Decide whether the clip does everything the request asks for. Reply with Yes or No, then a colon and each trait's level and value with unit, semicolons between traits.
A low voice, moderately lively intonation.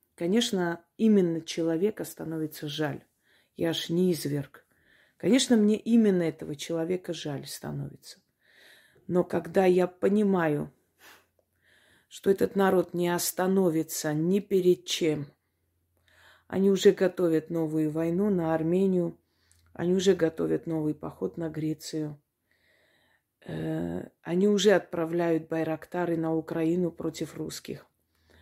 No: medium, 165 Hz; average, 3.0 semitones